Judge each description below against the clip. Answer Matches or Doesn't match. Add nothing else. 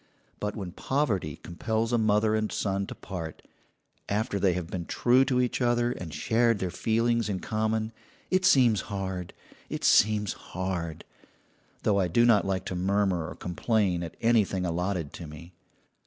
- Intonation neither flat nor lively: Matches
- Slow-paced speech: Doesn't match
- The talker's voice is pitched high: Doesn't match